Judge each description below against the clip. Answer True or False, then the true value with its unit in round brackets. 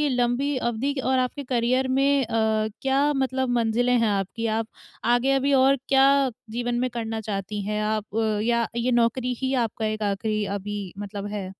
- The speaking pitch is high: True (240 Hz)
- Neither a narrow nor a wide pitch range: True (3.4 semitones)